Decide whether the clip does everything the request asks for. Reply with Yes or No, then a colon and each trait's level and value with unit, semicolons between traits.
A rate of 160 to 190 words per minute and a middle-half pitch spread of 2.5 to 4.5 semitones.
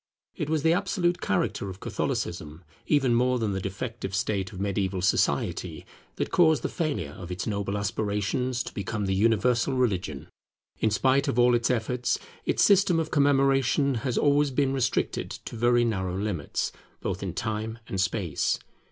No: average, 165 wpm; wide, 5.6 semitones